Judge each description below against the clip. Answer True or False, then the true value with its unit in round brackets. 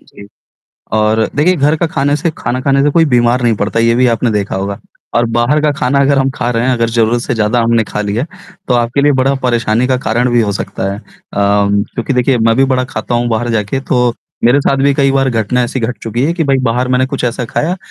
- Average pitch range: True (3.1 semitones)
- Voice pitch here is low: True (120 Hz)